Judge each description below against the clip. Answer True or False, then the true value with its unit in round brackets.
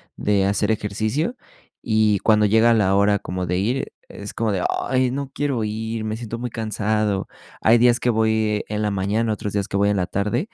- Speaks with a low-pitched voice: True (110 Hz)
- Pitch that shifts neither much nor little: False (2.2 semitones)